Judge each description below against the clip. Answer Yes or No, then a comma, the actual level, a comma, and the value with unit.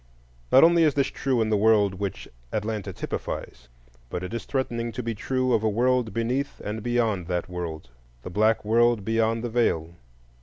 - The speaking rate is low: No, average, 180 wpm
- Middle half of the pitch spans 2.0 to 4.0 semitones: Yes, average, 3.4 semitones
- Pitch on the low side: Yes, low, 110 Hz